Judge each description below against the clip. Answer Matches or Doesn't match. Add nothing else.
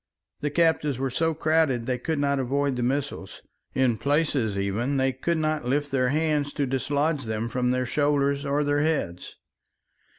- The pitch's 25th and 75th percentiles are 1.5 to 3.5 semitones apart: Matches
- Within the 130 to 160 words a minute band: Doesn't match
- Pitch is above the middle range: Doesn't match